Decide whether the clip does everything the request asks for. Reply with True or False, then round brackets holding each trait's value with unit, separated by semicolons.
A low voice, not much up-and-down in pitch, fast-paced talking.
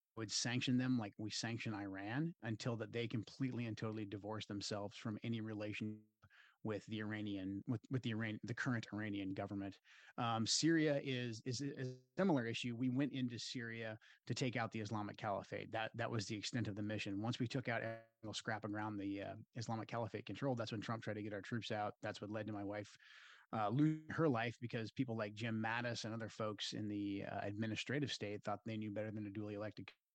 True (110 Hz; 2.3 semitones; 215 wpm)